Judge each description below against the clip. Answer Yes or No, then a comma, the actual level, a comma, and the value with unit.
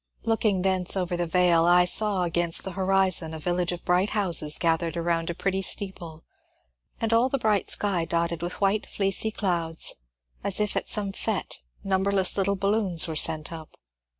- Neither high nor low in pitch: Yes, medium, 180 Hz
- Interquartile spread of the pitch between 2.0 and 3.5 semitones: Yes, average, 2.8 semitones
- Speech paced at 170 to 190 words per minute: Yes, average, 175 wpm